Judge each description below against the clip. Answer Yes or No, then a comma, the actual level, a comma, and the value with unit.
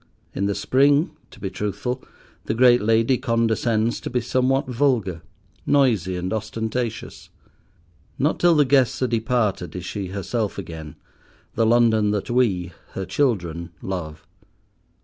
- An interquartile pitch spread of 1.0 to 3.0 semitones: No, average, 4.6 semitones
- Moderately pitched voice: No, low, 110 Hz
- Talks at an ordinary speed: No, slow, 130 wpm